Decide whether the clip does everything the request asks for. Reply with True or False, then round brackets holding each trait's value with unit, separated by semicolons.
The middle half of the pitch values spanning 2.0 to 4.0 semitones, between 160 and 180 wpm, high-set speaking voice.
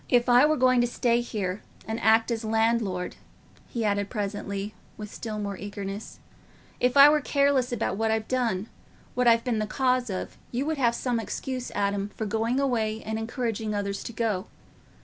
True (3.1 semitones; 175 wpm; 225 Hz)